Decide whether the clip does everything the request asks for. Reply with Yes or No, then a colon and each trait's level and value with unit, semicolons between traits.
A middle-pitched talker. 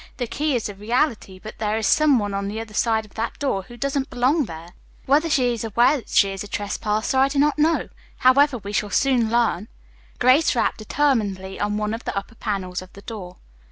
No: high, 225 Hz